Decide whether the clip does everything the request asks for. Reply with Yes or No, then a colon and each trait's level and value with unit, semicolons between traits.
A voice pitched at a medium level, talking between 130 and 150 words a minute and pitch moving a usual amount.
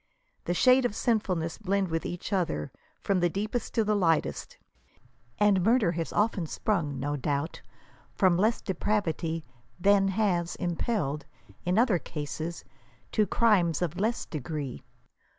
Yes: medium, 180 Hz; average, 140 wpm; average, 4.3 semitones